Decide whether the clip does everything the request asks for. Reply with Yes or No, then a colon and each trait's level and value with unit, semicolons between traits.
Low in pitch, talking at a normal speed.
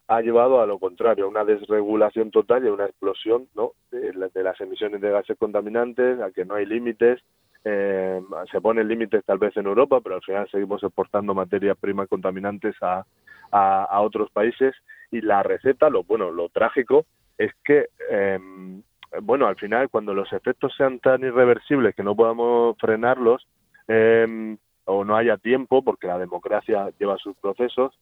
Yes: low, 115 Hz; average, 175 wpm